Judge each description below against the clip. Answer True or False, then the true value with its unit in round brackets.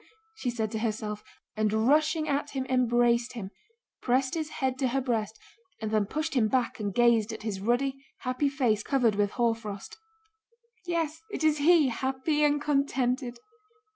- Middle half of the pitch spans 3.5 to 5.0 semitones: True (4.3 semitones)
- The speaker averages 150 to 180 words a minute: True (165 wpm)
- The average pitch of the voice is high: True (250 Hz)